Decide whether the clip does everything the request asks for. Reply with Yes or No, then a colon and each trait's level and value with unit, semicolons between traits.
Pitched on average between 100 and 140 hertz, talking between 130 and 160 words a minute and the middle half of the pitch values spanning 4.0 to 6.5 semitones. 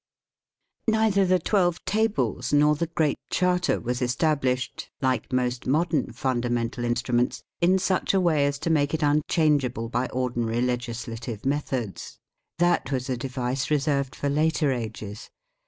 Yes: low, 135 Hz; average, 140 wpm; average, 4.5 semitones